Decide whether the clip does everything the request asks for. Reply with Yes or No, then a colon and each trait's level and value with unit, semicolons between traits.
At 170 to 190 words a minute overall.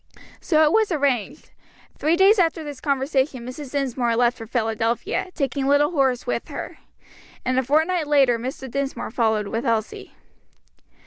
No: average, 150 wpm